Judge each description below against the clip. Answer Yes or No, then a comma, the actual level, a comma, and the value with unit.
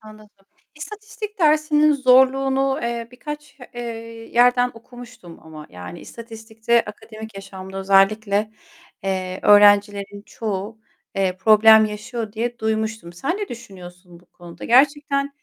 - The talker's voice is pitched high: Yes, high, 220 Hz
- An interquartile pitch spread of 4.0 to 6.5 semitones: Yes, average, 4.6 semitones